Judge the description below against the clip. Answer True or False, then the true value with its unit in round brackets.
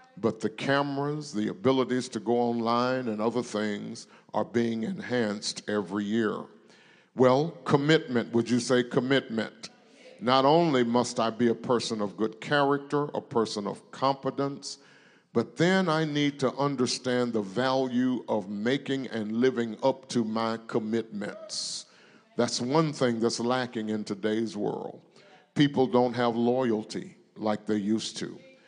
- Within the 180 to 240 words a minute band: False (140 wpm)